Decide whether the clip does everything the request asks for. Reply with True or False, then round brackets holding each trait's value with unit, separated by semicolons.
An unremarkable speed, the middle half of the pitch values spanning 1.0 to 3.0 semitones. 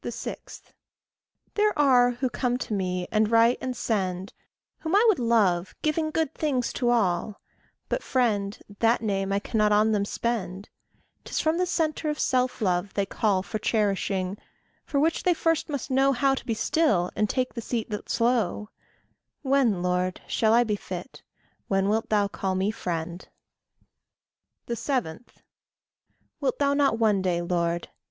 False (160 wpm; 5.2 semitones)